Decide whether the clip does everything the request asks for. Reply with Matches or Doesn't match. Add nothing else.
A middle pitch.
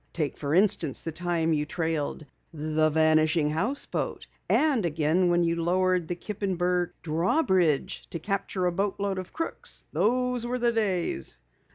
Matches